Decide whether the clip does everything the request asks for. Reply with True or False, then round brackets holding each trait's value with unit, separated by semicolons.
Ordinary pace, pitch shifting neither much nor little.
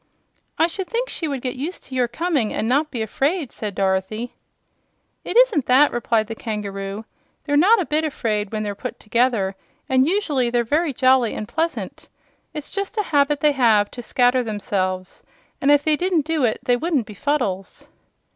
False (185 wpm; 5.9 semitones)